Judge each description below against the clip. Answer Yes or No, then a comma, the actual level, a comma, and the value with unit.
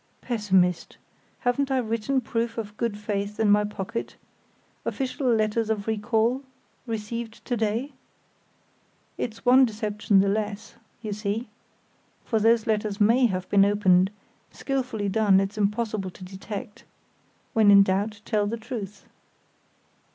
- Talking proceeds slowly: Yes, slow, 130 wpm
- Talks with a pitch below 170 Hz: No, high, 215 Hz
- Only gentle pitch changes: Yes, narrow, 2.2 semitones